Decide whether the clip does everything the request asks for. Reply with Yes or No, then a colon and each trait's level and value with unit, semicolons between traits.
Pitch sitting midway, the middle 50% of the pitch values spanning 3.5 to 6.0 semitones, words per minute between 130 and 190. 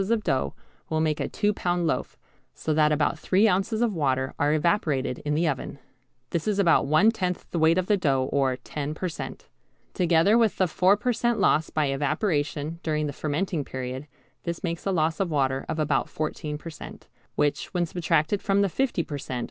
No: medium, 160 Hz; average, 4.1 semitones; fast, 205 wpm